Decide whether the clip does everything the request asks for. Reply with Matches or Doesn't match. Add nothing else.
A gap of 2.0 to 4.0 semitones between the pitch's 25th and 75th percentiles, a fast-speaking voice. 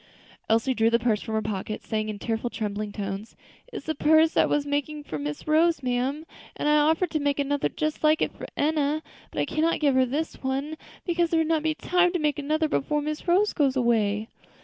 Doesn't match